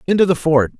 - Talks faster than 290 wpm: No, fast, 225 wpm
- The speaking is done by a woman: No, male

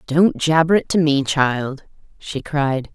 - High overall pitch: No, medium, 150 Hz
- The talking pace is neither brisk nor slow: Yes, average, 165 wpm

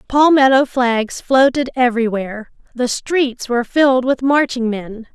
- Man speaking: No, female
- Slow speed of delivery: Yes, slow, 130 wpm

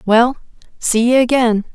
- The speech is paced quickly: No, average, 140 wpm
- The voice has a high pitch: Yes, high, 235 Hz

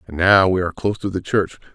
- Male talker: Yes, male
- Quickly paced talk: Yes, fast, 275 wpm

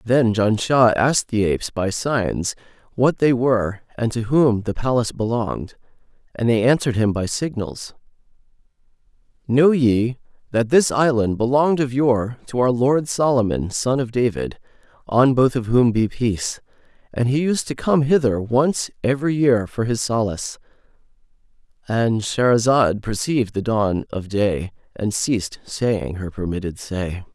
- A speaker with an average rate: Yes, average, 145 wpm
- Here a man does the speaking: Yes, male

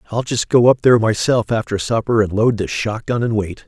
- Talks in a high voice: No, low, 110 Hz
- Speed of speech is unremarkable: No, fast, 245 wpm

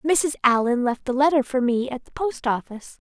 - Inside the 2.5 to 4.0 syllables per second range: No, 5.2 syllables/s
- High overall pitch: Yes, very high, 260 Hz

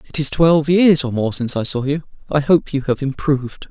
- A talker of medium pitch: Yes, medium, 145 Hz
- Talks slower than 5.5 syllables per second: No, 5.8 syllables/s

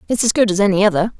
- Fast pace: Yes, fast, 350 wpm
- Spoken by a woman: Yes, female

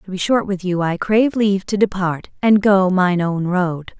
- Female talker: Yes, female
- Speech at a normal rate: No, fast, 225 wpm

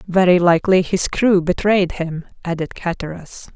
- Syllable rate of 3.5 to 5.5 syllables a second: Yes, 4.8 syllables/s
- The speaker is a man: No, female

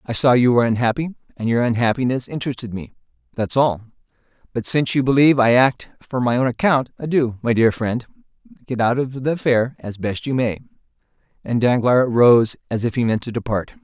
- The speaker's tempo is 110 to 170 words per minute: No, average, 190 wpm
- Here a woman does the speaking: No, male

